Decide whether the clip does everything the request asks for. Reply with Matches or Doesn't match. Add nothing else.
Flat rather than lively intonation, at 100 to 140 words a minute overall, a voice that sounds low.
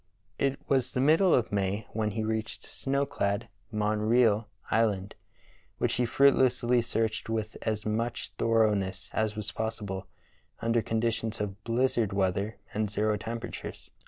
Matches